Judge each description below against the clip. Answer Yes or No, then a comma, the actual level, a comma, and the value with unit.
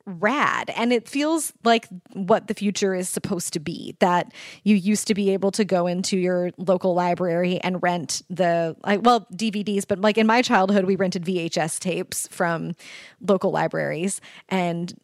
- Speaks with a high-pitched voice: Yes, high, 195 Hz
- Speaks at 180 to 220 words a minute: No, average, 170 wpm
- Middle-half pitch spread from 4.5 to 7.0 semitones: No, average, 3.0 semitones